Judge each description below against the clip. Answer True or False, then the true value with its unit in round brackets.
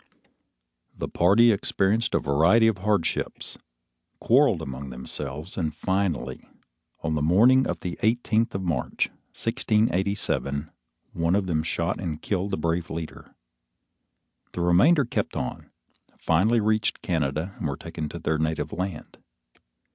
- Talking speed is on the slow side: True (130 wpm)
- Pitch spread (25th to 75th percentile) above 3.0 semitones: True (5.0 semitones)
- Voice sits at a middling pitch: False (90 Hz)